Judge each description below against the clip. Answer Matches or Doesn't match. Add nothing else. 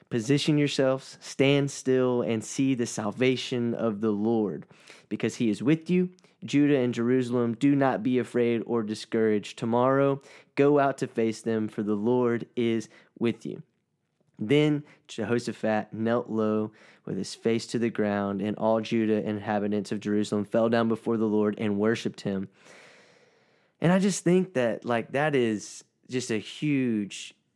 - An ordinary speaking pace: Matches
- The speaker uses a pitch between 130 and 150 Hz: Doesn't match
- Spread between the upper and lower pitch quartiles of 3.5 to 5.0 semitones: Matches